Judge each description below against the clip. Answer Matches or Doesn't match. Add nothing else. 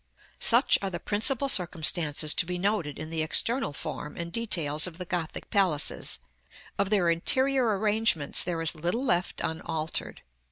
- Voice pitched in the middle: Matches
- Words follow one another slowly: Doesn't match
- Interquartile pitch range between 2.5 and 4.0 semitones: Doesn't match